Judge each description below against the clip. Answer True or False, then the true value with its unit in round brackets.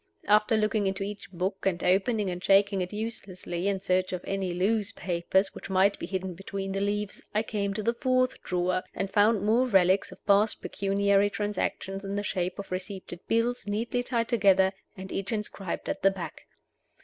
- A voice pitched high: True (195 Hz)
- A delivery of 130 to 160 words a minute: False (185 wpm)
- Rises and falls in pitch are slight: True (1.9 semitones)